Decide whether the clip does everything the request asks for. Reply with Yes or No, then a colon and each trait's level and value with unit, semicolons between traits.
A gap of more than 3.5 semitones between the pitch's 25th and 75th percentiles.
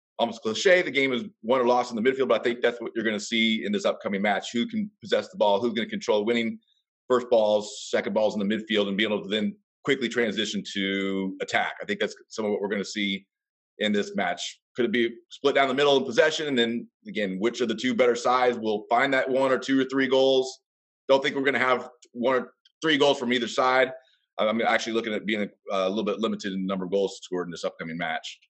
Yes: average, 4.0 semitones